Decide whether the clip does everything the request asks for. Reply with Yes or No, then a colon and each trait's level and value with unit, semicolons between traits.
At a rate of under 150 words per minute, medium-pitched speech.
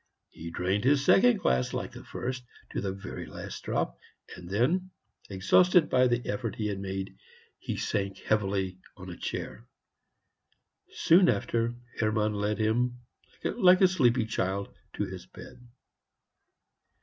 No: average, 140 wpm; low, 110 Hz